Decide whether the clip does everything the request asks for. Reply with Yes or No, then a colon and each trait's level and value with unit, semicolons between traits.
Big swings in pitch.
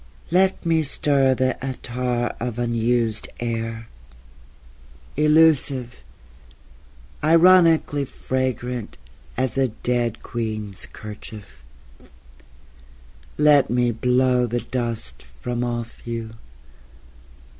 No: average, 2.7 semitones